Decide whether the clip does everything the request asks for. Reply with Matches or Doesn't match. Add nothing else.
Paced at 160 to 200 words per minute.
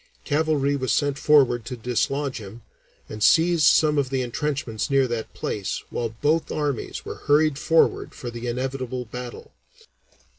Doesn't match